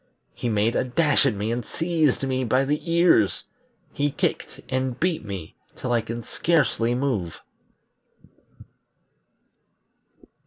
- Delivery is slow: Yes, slow, 125 wpm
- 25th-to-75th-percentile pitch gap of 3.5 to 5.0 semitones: Yes, average, 4.3 semitones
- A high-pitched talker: No, low, 130 Hz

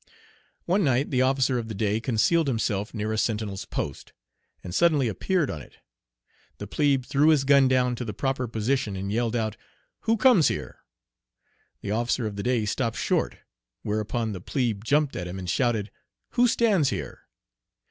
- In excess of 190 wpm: No, average, 175 wpm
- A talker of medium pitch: No, low, 120 Hz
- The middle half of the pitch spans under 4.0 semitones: No, average, 4.4 semitones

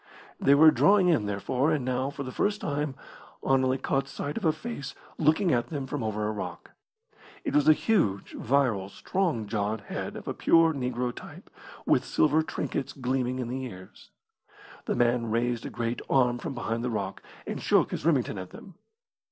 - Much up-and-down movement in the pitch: No, average, 4.2 semitones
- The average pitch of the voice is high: No, low, 130 Hz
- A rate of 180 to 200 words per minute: Yes, average, 185 wpm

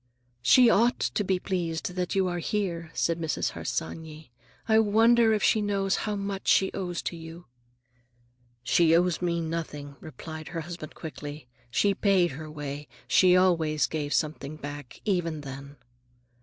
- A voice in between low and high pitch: Yes, medium, 170 Hz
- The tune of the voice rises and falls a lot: No, average, 3.9 semitones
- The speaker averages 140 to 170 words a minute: Yes, average, 155 wpm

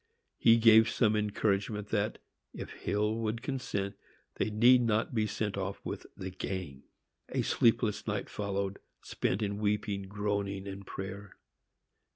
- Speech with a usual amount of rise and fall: No, narrow, 1.9 semitones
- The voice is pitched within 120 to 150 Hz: No, low, 105 Hz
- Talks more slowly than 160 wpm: Yes, average, 140 wpm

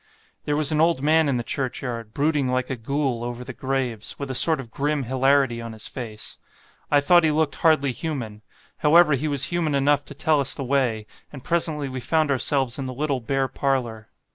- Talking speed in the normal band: No, fast, 210 wpm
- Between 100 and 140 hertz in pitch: Yes, low, 135 Hz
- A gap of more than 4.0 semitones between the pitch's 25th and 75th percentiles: No, average, 3.1 semitones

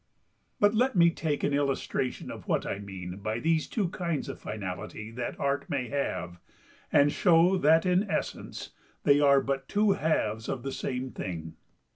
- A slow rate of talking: No, average, 170 wpm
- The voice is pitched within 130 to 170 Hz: Yes, medium, 140 Hz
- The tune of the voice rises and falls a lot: Yes, wide, 7.0 semitones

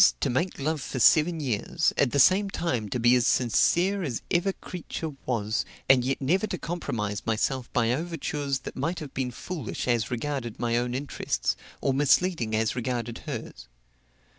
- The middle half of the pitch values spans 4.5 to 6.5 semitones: Yes, wide, 5.4 semitones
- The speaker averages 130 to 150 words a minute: No, average, 170 wpm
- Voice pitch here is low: Yes, low, 130 Hz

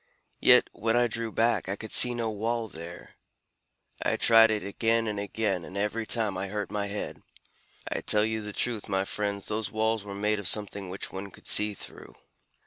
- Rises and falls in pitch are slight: Yes, narrow, 1.9 semitones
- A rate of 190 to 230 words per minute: Yes, average, 200 wpm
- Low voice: Yes, low, 105 Hz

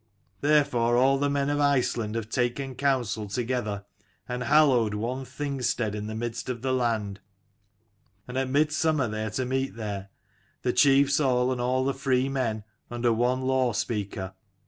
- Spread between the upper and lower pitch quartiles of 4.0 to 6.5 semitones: No, average, 3.0 semitones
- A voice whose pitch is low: Yes, low, 125 Hz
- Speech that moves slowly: No, average, 170 wpm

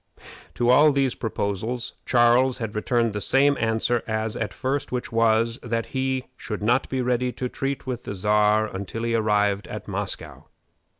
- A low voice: Yes, low, 115 Hz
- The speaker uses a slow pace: No, average, 170 wpm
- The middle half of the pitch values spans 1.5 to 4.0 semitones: Yes, average, 2.8 semitones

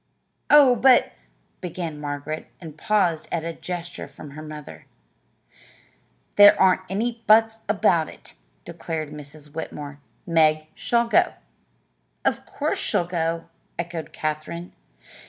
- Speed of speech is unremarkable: No, slow, 120 wpm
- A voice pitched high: No, medium, 165 Hz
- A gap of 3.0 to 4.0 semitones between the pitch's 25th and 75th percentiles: No, average, 4.7 semitones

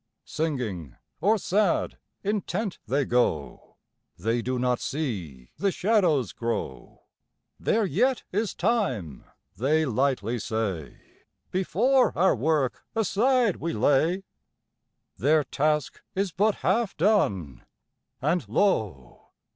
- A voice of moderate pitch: Yes, medium, 150 Hz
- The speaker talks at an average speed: No, slow, 105 wpm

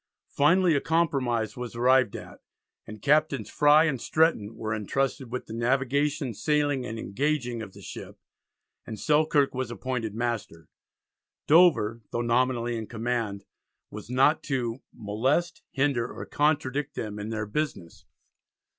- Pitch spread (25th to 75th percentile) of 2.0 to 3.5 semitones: No, average, 4.5 semitones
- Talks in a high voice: No, low, 125 Hz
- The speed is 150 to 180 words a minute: No, slow, 135 wpm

